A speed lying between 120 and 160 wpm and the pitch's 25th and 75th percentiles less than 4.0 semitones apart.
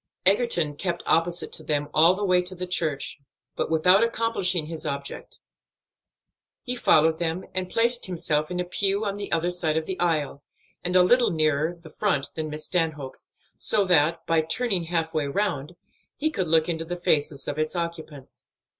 No: average, 185 wpm; average, 3.0 semitones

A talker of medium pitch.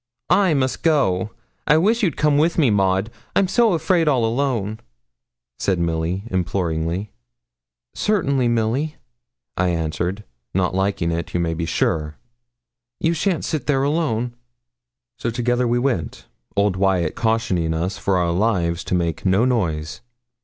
No: low, 105 Hz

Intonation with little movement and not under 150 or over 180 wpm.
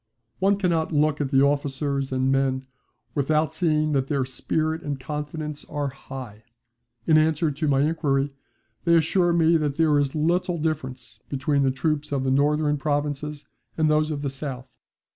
Yes: narrow, 2.3 semitones; average, 165 wpm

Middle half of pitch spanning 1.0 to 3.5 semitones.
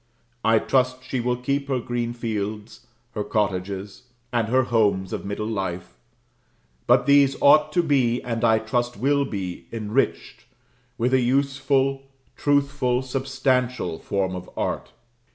No: average, 3.9 semitones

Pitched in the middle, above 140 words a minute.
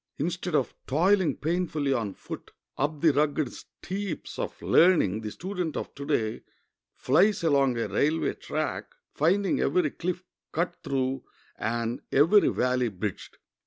No: medium, 150 Hz; slow, 135 wpm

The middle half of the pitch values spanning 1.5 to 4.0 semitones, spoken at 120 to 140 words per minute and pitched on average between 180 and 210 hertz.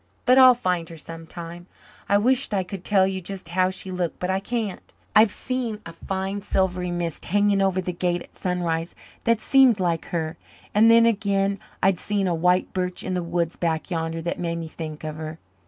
No: average, 3.0 semitones; fast, 205 wpm; medium, 185 Hz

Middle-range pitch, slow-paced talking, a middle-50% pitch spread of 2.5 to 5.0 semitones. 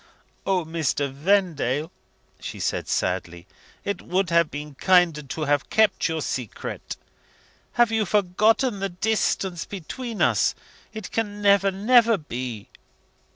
No: medium, 180 Hz; slow, 125 wpm; wide, 5.6 semitones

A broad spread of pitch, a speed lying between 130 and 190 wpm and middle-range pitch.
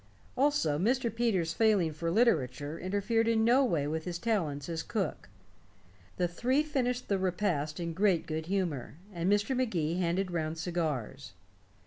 Yes: wide, 6.0 semitones; average, 150 wpm; medium, 180 Hz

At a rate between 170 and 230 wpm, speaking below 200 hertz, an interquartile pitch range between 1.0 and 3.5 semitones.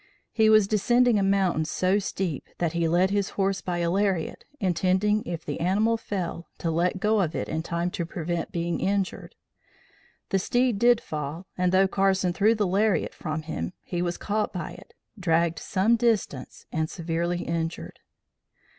Yes: average, 175 wpm; medium, 185 Hz; average, 3.1 semitones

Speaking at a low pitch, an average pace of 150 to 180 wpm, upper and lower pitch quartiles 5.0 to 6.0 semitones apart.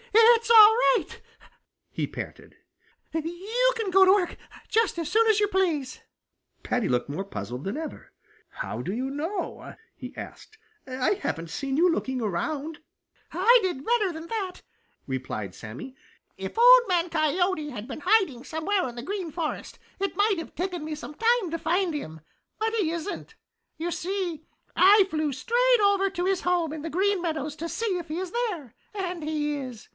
No: very high, 345 Hz; average, 175 wpm; wide, 5.5 semitones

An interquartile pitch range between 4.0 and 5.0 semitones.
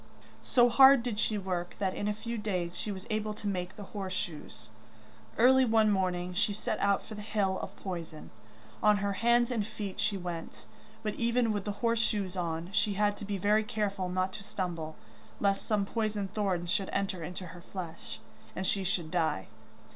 No: average, 2.8 semitones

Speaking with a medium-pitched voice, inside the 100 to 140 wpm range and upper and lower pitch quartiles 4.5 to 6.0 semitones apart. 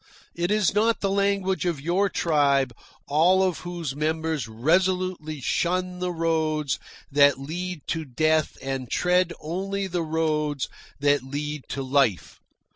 No: medium, 160 Hz; slow, 135 wpm; average, 4.1 semitones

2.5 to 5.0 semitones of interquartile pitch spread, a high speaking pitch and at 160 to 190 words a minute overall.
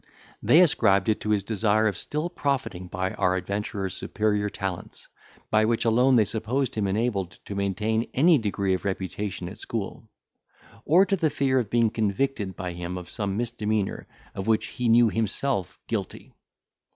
No: average, 3.6 semitones; low, 105 Hz; average, 165 wpm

